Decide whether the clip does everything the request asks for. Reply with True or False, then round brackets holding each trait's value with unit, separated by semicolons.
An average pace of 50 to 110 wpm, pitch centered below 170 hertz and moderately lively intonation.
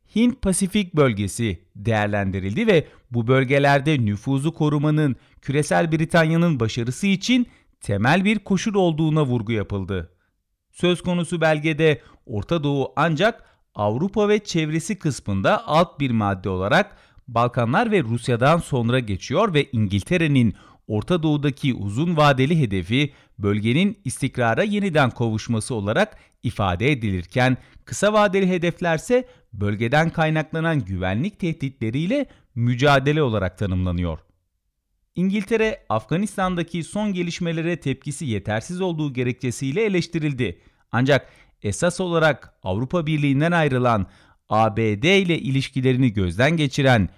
False (105 wpm; 140 Hz; 7.4 semitones)